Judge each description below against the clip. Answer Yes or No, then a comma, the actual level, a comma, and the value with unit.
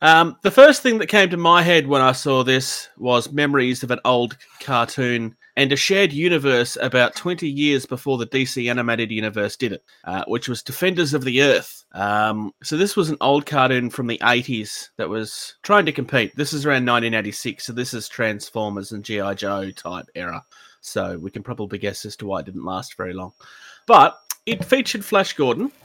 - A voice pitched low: Yes, low, 125 Hz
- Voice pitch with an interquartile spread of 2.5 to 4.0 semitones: No, average, 5.2 semitones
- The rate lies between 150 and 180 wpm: No, average, 200 wpm